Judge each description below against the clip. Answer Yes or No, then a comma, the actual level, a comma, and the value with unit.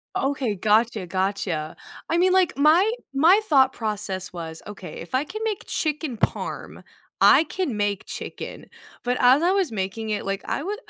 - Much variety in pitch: Yes, wide, 8.3 semitones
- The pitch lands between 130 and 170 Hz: No, high, 245 Hz